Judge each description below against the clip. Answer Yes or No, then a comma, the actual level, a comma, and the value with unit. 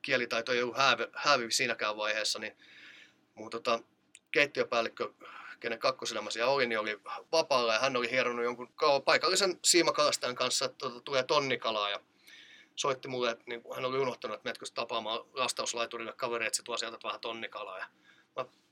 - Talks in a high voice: No, low, 120 Hz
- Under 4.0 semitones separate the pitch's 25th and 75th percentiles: Yes, average, 2.7 semitones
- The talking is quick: No, average, 145 wpm